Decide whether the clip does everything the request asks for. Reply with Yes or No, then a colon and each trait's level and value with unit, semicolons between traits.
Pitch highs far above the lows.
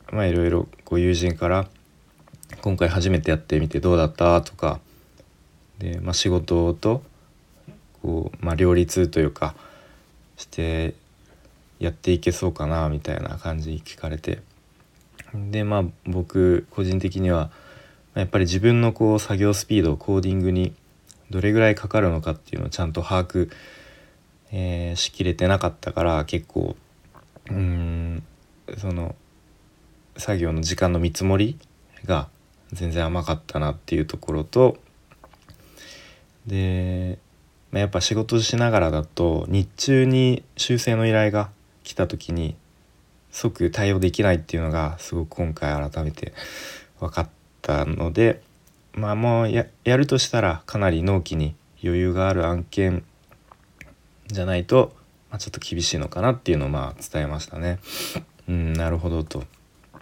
No: average, 3.7 semitones